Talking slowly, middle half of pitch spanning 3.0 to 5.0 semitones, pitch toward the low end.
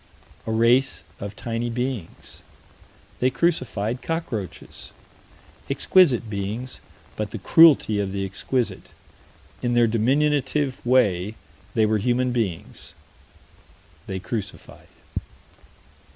Yes: slow, 95 wpm; average, 3.7 semitones; low, 115 Hz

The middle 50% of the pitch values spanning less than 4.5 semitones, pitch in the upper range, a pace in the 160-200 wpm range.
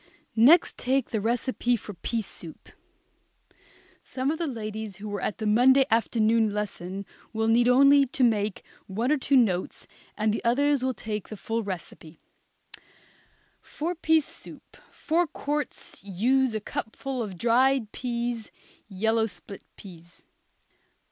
No: average, 4.0 semitones; high, 230 Hz; average, 140 wpm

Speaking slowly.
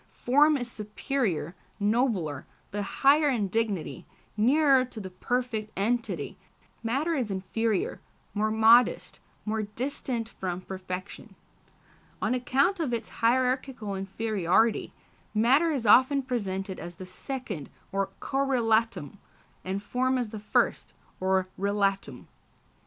Yes: slow, 115 wpm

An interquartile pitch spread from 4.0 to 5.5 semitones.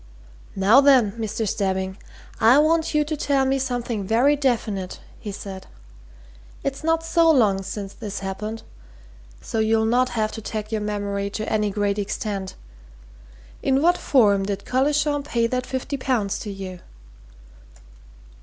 Yes: average, 5.1 semitones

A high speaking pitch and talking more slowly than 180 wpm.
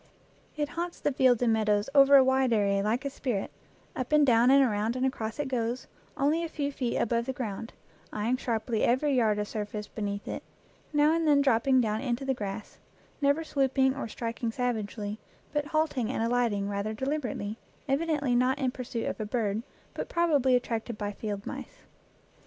No: high, 245 Hz; average, 185 wpm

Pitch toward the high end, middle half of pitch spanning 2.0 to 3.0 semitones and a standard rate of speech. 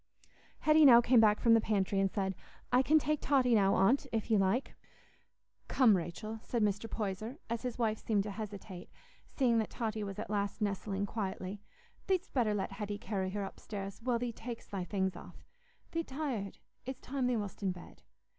No: high, 215 Hz; average, 3.7 semitones; average, 190 wpm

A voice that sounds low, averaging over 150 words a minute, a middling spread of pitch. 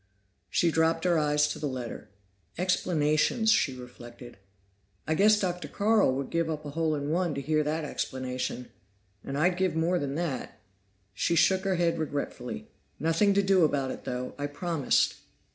No: medium, 155 Hz; average, 170 wpm; average, 4.1 semitones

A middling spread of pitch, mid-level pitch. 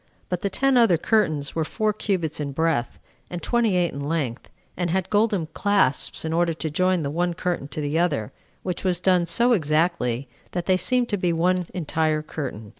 Yes: average, 3.4 semitones; medium, 170 Hz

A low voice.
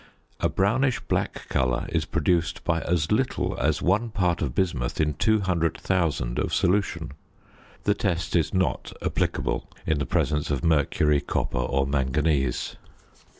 Yes: very low, 80 Hz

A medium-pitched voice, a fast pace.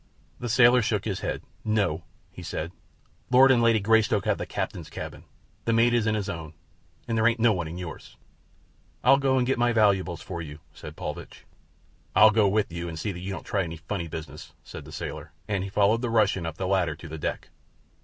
No: low, 105 Hz; fast, 220 wpm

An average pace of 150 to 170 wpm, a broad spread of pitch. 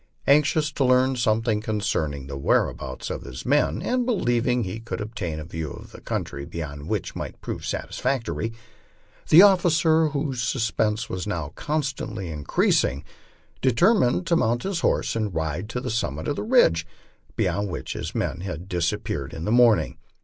Yes: average, 165 wpm; wide, 8.8 semitones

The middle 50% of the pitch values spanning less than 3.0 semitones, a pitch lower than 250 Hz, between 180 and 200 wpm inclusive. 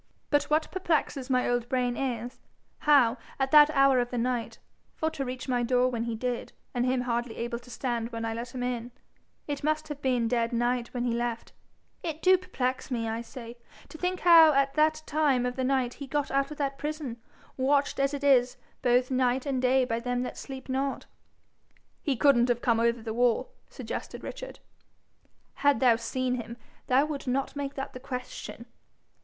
No: narrow, 2.5 semitones; very high, 255 Hz; average, 195 wpm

